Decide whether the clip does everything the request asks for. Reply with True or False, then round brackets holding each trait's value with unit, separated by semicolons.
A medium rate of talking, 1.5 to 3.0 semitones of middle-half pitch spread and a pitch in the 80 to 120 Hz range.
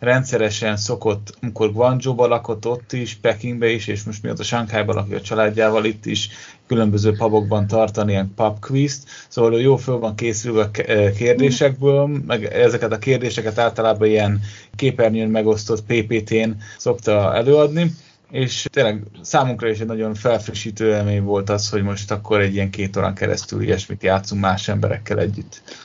True (145 wpm; 2.4 semitones; 110 Hz)